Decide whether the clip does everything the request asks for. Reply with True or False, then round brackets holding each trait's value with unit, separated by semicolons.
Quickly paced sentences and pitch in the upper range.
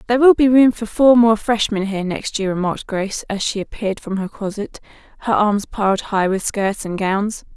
True (215 wpm; 210 Hz)